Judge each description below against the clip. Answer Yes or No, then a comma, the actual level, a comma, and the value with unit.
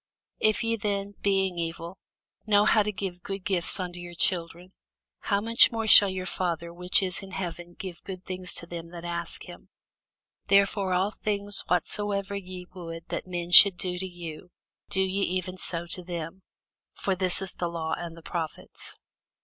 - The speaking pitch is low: No, medium, 185 Hz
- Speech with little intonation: Yes, narrow, 2.3 semitones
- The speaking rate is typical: Yes, average, 180 wpm